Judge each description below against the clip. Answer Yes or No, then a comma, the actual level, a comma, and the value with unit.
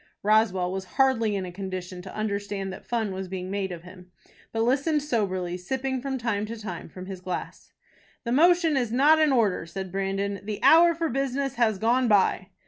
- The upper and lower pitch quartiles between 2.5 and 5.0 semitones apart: No, wide, 5.6 semitones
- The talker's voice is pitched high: Yes, high, 210 Hz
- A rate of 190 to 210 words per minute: Yes, average, 195 wpm